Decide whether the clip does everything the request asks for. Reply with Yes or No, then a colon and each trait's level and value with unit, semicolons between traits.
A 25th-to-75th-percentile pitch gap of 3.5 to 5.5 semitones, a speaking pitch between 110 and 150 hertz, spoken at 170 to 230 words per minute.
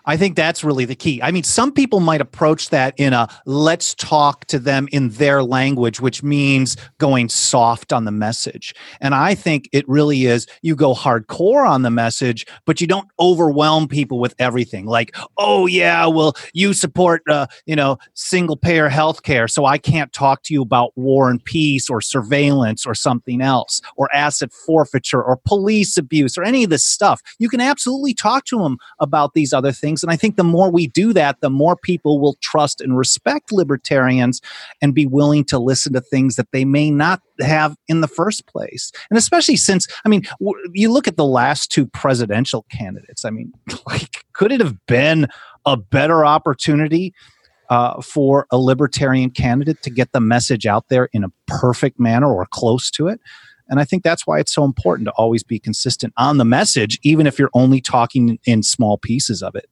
Yes: average, 4.2 semitones; medium, 140 Hz; average, 200 wpm